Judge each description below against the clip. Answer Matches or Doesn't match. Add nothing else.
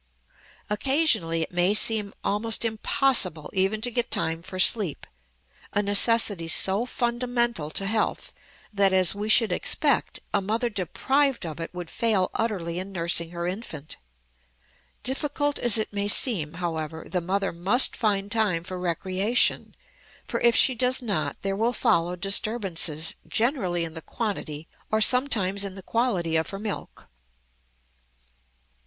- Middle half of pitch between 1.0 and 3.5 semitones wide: Doesn't match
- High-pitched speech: Matches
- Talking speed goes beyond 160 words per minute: Doesn't match